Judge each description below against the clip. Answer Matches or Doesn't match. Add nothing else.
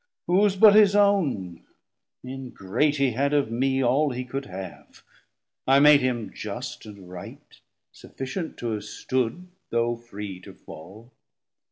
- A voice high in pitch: Doesn't match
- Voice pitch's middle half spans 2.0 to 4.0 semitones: Doesn't match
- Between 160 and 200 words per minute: Doesn't match